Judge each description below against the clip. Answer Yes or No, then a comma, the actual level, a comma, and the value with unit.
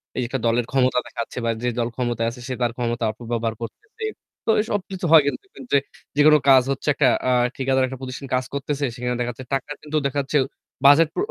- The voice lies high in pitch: No, low, 130 Hz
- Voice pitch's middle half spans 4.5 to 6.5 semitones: No, average, 3.2 semitones